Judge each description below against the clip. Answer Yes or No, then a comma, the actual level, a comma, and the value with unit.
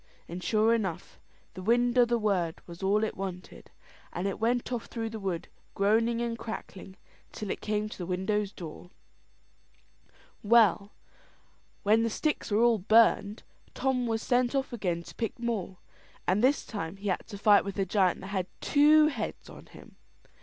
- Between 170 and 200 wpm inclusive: Yes, average, 175 wpm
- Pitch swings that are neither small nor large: Yes, average, 3.4 semitones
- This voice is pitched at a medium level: No, high, 210 Hz